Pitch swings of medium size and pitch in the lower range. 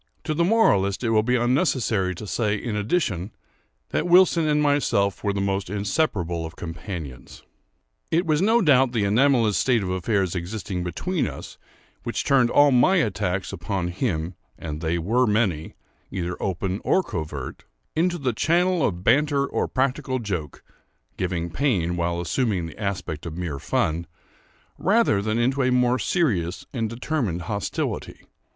No: wide, 7.3 semitones; low, 105 Hz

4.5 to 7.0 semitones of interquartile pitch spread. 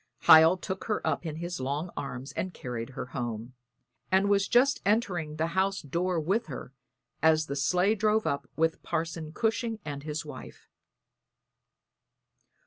Yes: wide, 5.4 semitones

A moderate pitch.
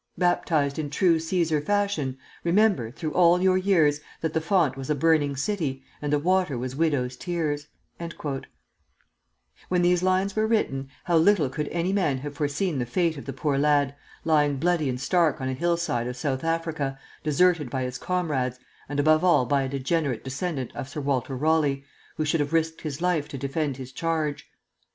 Yes: medium, 150 Hz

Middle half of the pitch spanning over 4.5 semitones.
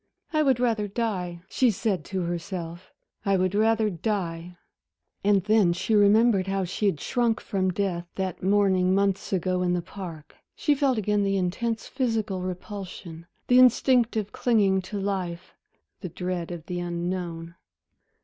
No: average, 3.3 semitones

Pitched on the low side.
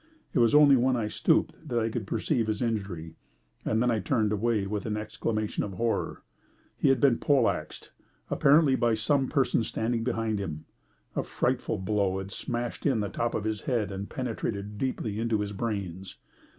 Yes: low, 110 Hz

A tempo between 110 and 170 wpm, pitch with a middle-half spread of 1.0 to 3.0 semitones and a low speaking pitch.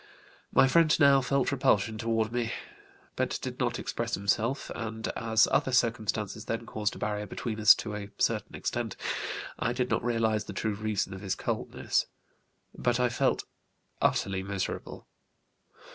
Yes: average, 155 wpm; narrow, 2.6 semitones; low, 110 Hz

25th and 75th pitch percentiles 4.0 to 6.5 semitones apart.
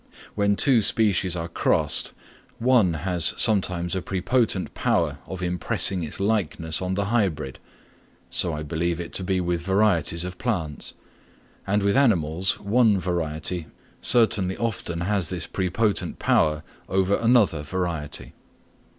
No: average, 3.3 semitones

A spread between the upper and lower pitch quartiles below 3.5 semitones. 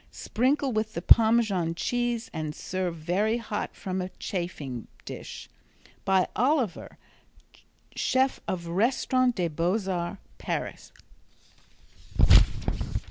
No: wide, 5.4 semitones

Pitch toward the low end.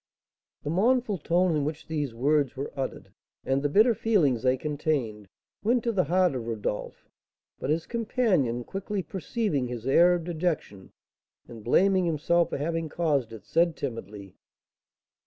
No: medium, 155 Hz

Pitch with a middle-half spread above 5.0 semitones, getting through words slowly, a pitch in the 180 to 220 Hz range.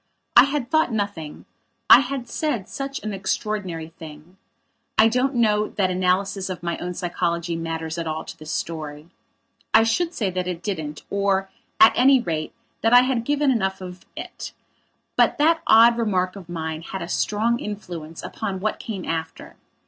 No: wide, 5.4 semitones; average, 170 wpm; high, 190 Hz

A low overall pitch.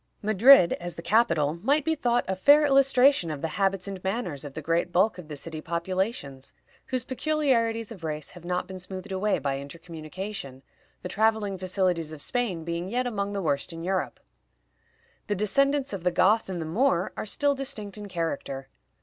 No: high, 190 Hz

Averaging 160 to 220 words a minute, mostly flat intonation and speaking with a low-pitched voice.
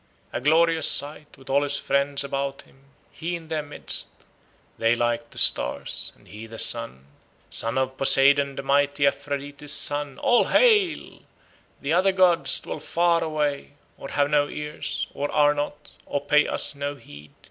No: average, 165 wpm; narrow, 1.7 semitones; medium, 145 Hz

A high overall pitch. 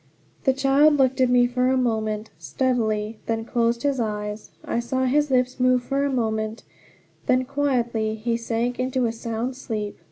Yes: high, 245 Hz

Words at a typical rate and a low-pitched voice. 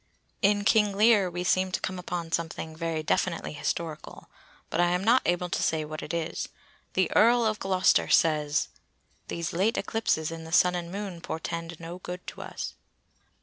No: average, 180 wpm; medium, 175 Hz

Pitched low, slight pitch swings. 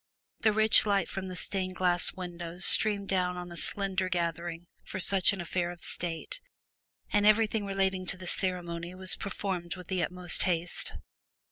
No: medium, 185 Hz; narrow, 1.9 semitones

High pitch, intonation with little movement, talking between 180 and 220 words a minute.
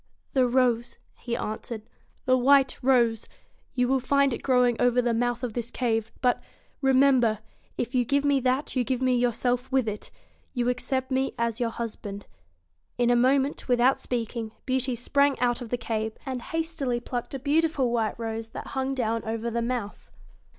Yes: high, 245 Hz; narrow, 2.1 semitones; average, 185 wpm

